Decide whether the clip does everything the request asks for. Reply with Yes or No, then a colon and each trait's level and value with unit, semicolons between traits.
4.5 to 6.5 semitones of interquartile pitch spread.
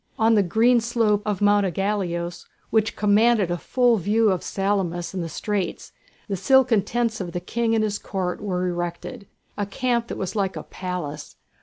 No: average, 3.7 semitones